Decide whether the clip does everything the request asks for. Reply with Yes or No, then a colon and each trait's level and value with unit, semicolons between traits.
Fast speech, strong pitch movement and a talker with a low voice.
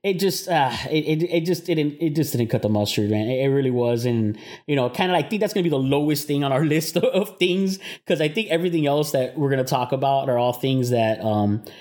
No: fast, 285 wpm; wide, 5.7 semitones; medium, 145 Hz